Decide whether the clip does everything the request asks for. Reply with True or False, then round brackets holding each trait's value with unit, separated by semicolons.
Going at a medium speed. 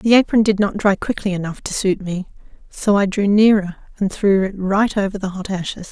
False (225 wpm)